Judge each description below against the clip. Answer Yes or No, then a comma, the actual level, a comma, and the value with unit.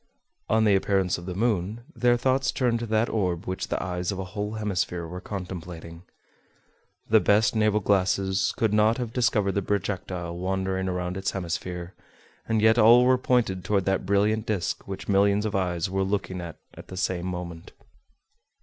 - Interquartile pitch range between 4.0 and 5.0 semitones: No, average, 3.0 semitones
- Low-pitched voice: Yes, very low, 95 Hz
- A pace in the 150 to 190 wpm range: Yes, average, 175 wpm